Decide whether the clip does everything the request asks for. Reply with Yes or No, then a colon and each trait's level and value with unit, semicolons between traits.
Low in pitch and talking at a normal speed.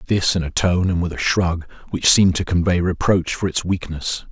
No: very low, 90 Hz; fast, 225 wpm